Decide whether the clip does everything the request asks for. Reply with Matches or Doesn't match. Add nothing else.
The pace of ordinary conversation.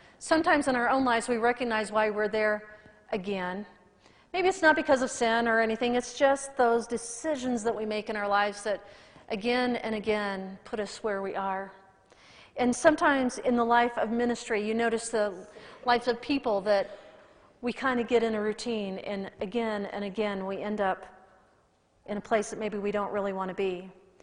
Matches